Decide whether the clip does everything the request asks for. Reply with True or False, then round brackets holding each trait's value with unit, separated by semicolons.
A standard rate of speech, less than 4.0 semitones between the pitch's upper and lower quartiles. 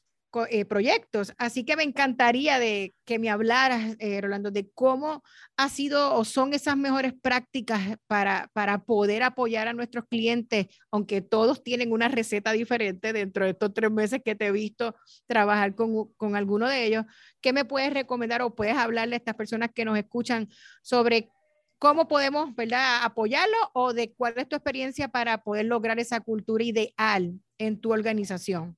True (170 wpm; 2.9 semitones)